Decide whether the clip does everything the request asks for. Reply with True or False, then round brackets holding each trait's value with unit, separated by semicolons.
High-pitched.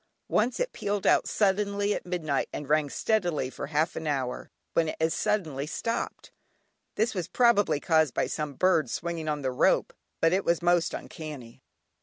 False (165 Hz)